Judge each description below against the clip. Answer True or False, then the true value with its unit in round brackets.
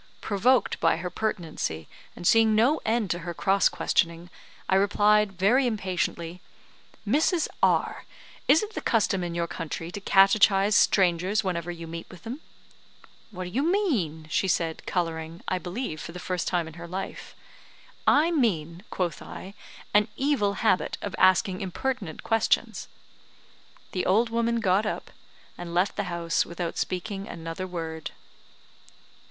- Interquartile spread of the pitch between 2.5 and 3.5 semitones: False (4.2 semitones)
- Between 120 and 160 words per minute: True (150 wpm)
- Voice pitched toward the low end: False (185 Hz)